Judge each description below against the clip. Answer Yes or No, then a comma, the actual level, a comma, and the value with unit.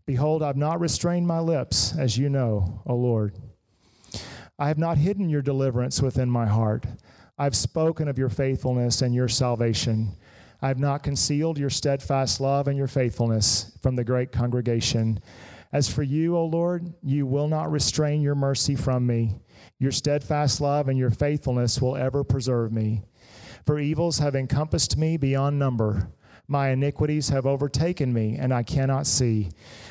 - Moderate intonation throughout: Yes, average, 3.5 semitones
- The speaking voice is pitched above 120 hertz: Yes, low, 135 Hz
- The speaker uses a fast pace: No, average, 160 wpm